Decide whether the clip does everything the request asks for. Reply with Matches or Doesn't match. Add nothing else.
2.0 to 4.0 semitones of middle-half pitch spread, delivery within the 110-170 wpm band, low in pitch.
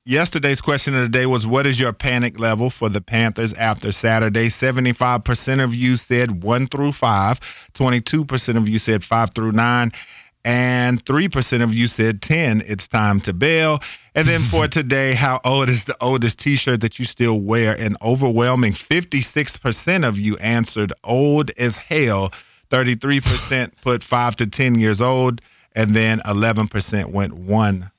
Matches